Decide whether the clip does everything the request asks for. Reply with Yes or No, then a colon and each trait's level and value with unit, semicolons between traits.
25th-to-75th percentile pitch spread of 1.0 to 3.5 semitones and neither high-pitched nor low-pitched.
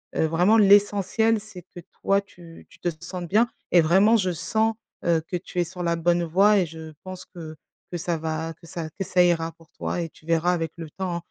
Yes: average, 2.8 semitones; medium, 175 Hz